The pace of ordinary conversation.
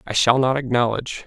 Yes: average, 190 wpm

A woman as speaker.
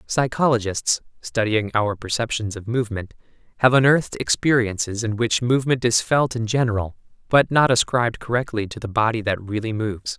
No: male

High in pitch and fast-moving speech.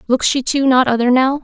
Yes: very high, 260 Hz; fast, 250 wpm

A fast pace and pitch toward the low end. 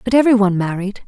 No: fast, 225 wpm; high, 210 Hz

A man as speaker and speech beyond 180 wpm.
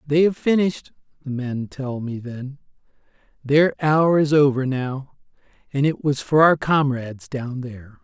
No: male; average, 155 wpm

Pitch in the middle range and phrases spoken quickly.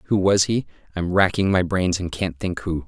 No: very low, 90 Hz; fast, 230 wpm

